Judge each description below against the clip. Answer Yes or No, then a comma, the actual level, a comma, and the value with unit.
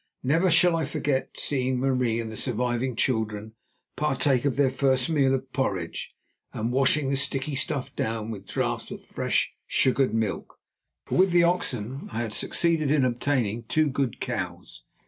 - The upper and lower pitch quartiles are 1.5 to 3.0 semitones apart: No, average, 3.5 semitones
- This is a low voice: Yes, low, 130 Hz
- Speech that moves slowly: No, average, 165 wpm